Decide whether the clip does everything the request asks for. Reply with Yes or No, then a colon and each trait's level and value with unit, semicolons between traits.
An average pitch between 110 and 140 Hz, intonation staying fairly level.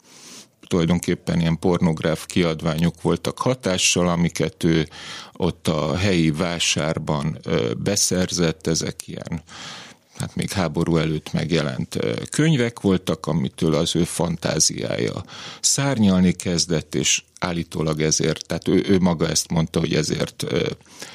No: very low, 85 Hz; narrow, 2.2 semitones